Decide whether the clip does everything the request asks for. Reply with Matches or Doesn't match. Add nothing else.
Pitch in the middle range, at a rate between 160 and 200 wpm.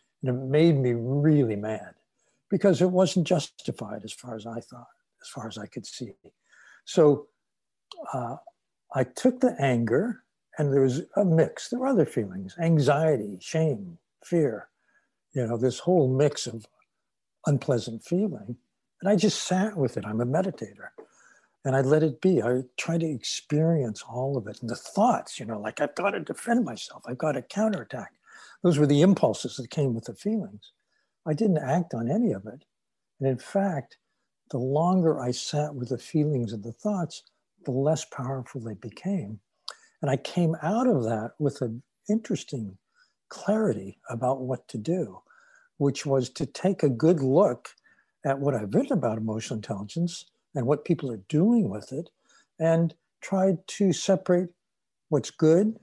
Matches